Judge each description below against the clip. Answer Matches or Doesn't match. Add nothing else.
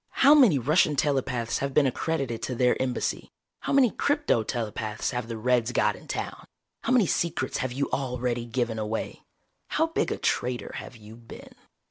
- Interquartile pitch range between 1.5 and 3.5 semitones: Doesn't match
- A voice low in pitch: Matches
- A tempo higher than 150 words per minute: Matches